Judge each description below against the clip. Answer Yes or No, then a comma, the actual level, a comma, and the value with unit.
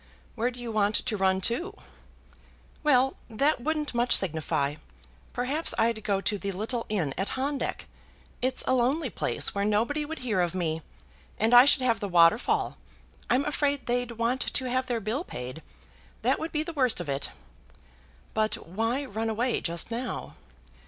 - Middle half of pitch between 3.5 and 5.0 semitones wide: Yes, average, 4.5 semitones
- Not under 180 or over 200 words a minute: No, average, 170 wpm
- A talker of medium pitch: No, high, 235 Hz